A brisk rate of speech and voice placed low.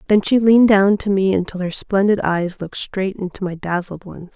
No: fast, 220 wpm; high, 190 Hz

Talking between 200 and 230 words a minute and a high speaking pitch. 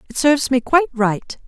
Yes: fast, 205 wpm; very high, 260 Hz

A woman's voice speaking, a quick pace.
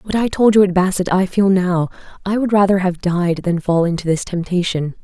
Yes: female; fast, 225 wpm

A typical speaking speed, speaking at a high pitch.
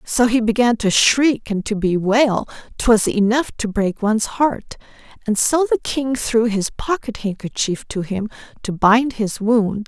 Yes: average, 170 wpm; high, 225 Hz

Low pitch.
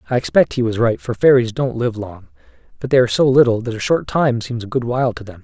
Yes: low, 115 Hz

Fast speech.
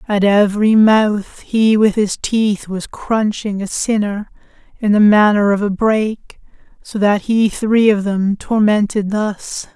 No: average, 155 wpm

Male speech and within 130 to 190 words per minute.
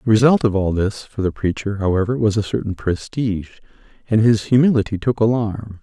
Yes: male; average, 185 wpm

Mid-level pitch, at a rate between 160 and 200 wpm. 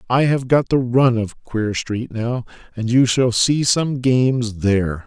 No: low, 120 Hz; average, 190 wpm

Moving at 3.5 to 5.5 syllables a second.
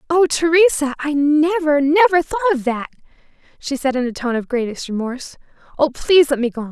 No: 5.8 syllables/s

